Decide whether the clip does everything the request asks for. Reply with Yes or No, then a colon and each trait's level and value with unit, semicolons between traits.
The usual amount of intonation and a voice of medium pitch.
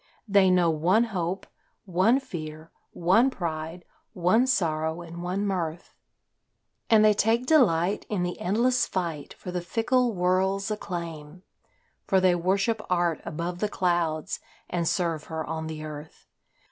Yes: average, 3.6 semitones; medium, 180 Hz